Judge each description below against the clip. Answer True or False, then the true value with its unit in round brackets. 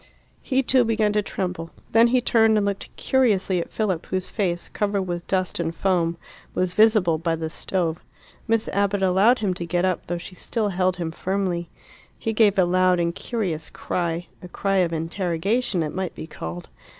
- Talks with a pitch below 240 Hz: True (185 Hz)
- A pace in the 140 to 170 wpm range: False (185 wpm)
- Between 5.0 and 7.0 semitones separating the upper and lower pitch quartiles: False (3.4 semitones)